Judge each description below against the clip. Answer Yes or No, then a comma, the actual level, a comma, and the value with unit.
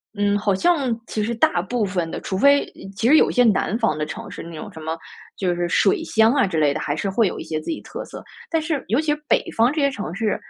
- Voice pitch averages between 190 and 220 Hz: Yes, high, 215 Hz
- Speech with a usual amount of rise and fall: No, wide, 7.7 semitones